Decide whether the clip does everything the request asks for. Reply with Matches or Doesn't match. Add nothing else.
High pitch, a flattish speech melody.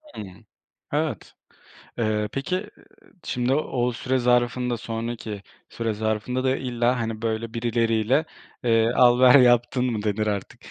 Doesn't match